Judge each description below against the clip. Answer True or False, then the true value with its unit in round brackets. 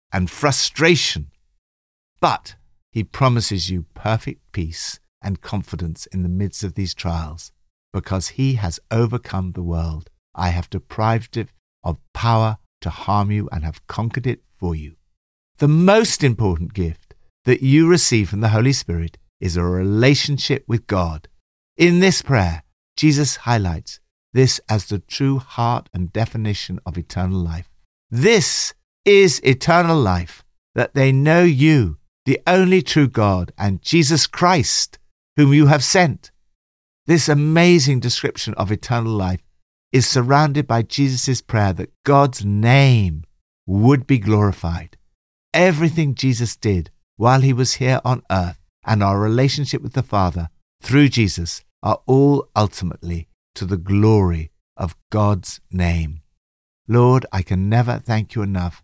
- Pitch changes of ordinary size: False (7.2 semitones)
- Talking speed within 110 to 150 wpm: True (140 wpm)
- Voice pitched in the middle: False (105 Hz)